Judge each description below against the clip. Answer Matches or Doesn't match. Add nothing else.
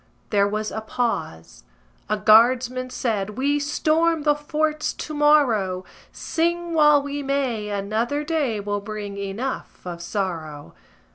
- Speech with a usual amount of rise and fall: Doesn't match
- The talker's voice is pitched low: Doesn't match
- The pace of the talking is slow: Matches